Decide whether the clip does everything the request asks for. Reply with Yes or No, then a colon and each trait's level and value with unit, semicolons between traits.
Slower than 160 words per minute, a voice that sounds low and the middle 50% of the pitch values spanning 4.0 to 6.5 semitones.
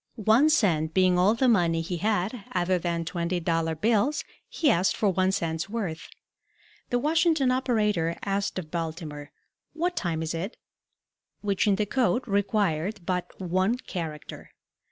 No: average, 150 wpm; medium, 185 Hz; average, 4.7 semitones